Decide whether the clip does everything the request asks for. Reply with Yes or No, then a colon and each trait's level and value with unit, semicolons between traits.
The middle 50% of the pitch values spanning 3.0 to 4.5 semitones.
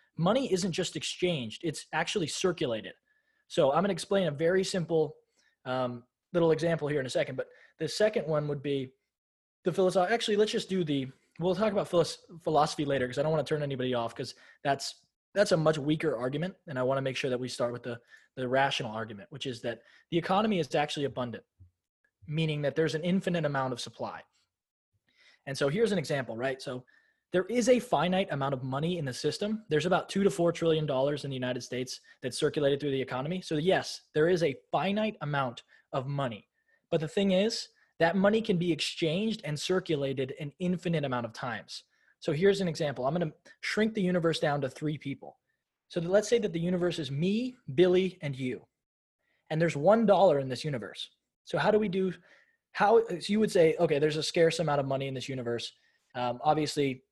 No: average, 5.3 semitones